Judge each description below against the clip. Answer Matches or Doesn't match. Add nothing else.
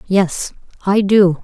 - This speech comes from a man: Doesn't match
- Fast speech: Doesn't match